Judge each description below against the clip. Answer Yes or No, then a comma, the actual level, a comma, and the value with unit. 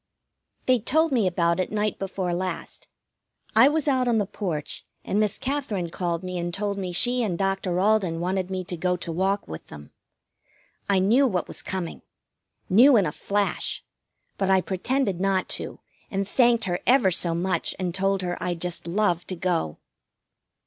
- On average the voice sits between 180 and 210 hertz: Yes, high, 190 Hz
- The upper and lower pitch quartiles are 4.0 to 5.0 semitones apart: No, average, 3.2 semitones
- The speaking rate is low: No, average, 180 wpm